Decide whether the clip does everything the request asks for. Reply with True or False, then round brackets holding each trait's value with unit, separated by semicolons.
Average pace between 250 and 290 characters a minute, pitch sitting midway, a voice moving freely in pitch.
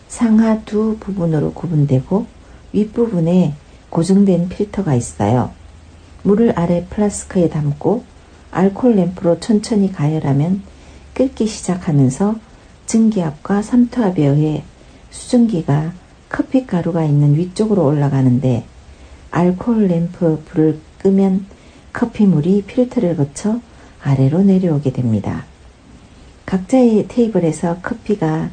True (260 characters per minute; 175 Hz; 6.3 semitones)